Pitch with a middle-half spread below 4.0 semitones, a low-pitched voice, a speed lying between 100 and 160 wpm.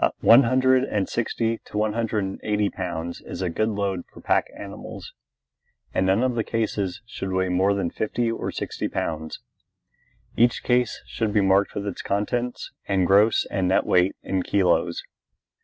No: average, 3.3 semitones; low, 100 Hz; average, 175 wpm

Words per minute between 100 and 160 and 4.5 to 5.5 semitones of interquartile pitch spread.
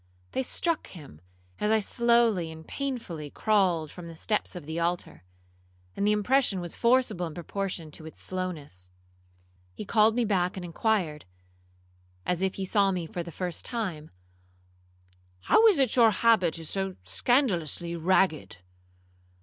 Yes: average, 150 wpm; average, 5.0 semitones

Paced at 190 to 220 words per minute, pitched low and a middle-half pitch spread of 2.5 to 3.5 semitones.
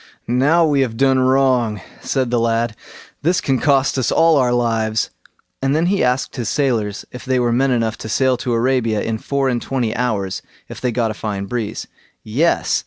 Yes: average, 195 wpm; low, 125 Hz; average, 2.9 semitones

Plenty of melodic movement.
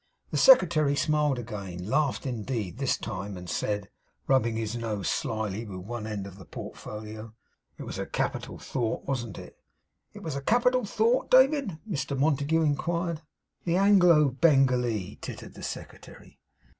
Yes: wide, 6.6 semitones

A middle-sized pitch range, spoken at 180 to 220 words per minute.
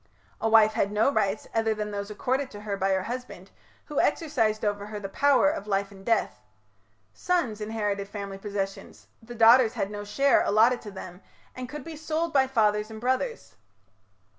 Yes: average, 3.9 semitones; average, 185 wpm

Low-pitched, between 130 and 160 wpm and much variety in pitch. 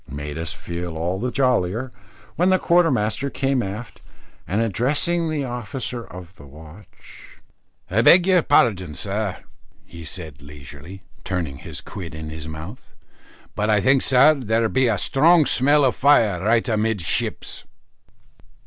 Yes: low, 110 Hz; average, 150 wpm; wide, 7.3 semitones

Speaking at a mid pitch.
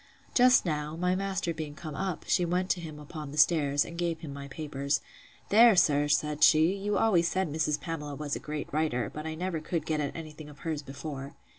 Yes: medium, 155 Hz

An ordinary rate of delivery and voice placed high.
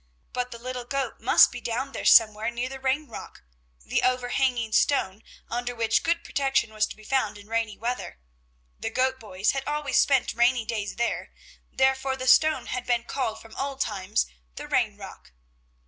Yes: average, 180 wpm; high, 245 Hz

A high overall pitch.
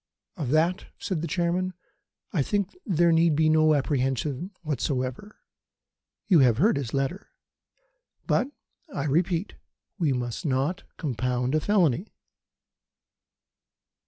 No: medium, 155 Hz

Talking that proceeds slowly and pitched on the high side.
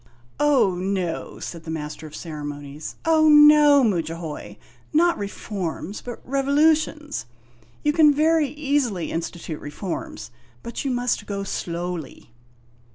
Yes: slow, 115 wpm; high, 210 Hz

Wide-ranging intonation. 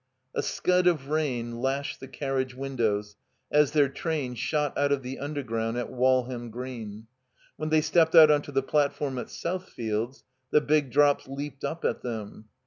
No: average, 3.4 semitones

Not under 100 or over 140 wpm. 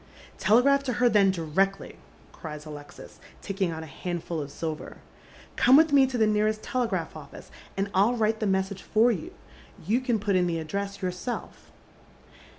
No: average, 175 wpm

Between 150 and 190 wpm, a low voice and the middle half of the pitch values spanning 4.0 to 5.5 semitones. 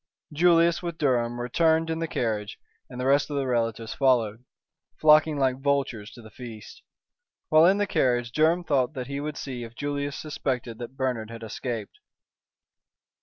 Yes: average, 165 wpm; low, 130 Hz; average, 4.5 semitones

